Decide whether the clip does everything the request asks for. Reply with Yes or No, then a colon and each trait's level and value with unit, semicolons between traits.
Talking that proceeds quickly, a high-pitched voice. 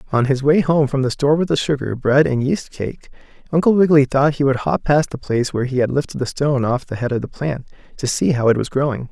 No: fast, 270 wpm; medium, 140 Hz